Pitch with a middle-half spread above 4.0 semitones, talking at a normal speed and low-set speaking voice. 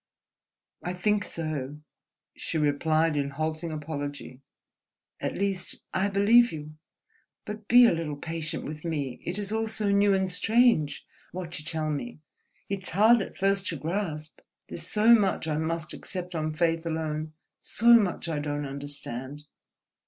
No: average, 4.6 semitones; average, 150 wpm; medium, 165 Hz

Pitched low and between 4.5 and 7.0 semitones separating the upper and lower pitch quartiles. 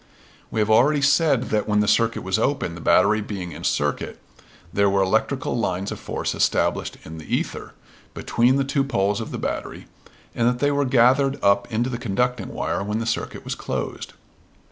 Yes: low, 115 Hz; average, 4.8 semitones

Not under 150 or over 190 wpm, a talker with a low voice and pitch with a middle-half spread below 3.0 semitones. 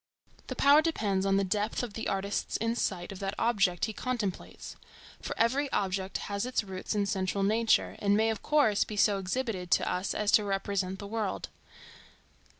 No: average, 180 wpm; high, 205 Hz; narrow, 2.6 semitones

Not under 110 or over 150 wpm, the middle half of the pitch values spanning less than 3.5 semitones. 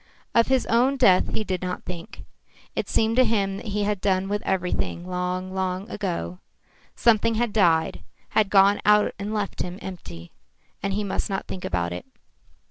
No: average, 180 wpm; narrow, 2.5 semitones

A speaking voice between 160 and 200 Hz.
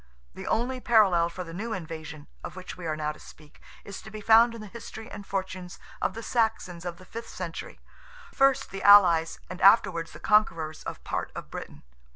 Yes: medium, 185 Hz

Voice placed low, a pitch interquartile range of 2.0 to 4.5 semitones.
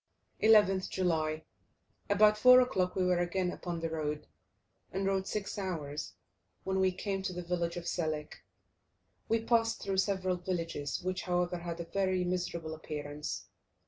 No: medium, 180 Hz; narrow, 2.5 semitones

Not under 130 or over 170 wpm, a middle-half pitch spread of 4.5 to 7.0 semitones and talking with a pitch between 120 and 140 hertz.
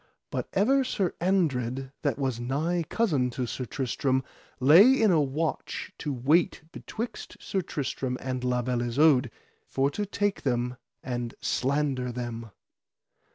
Yes: average, 140 wpm; average, 5.2 semitones; low, 135 Hz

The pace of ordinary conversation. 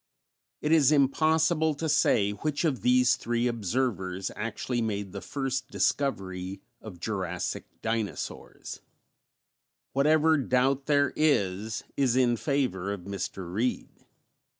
No: slow, 115 wpm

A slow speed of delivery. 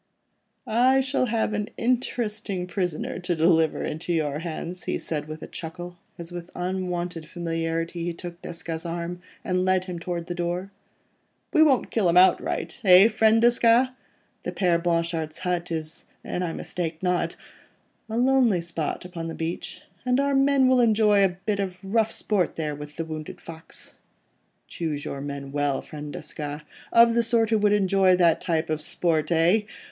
No: average, 165 wpm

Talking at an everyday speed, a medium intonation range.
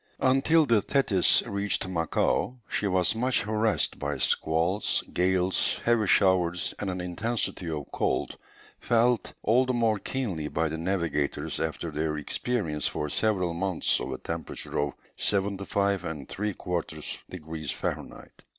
No: slow, 130 wpm; average, 5.0 semitones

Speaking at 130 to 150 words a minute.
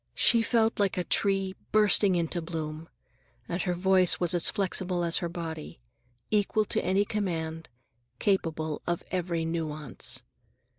Yes: average, 140 wpm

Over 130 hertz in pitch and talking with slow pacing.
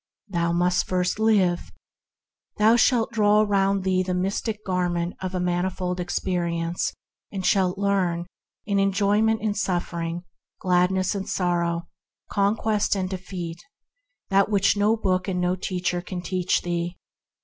Yes: medium, 185 Hz; slow, 130 wpm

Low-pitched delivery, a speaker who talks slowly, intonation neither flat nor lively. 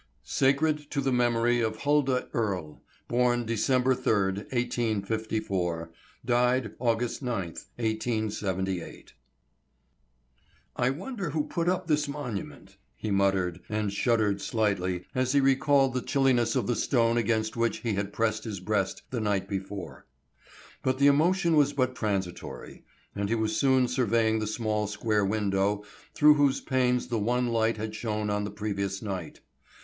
No: low, 115 Hz; average, 145 wpm; average, 3.9 semitones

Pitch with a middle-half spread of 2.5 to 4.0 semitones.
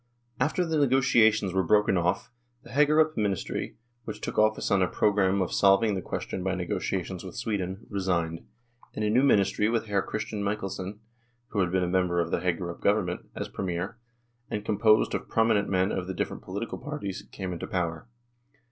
Yes: average, 2.9 semitones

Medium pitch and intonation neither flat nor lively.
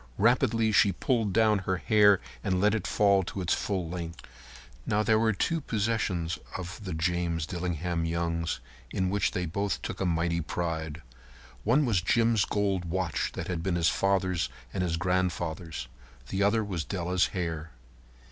No: very low, 95 Hz; average, 3.3 semitones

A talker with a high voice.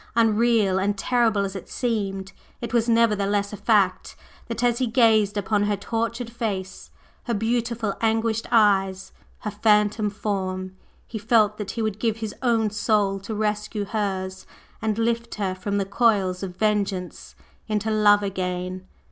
Yes: high, 210 Hz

